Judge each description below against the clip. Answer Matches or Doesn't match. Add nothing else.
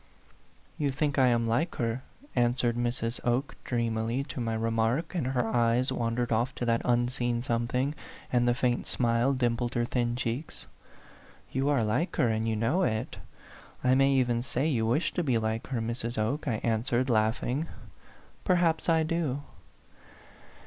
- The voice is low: Matches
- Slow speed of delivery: Doesn't match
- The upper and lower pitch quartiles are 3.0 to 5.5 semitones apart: Doesn't match